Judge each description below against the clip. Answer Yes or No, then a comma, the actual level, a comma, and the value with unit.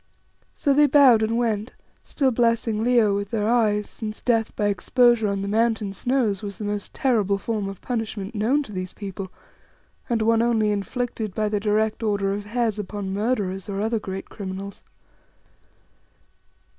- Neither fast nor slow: Yes, average, 165 wpm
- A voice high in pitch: Yes, high, 215 Hz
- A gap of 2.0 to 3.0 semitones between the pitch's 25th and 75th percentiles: Yes, narrow, 2.6 semitones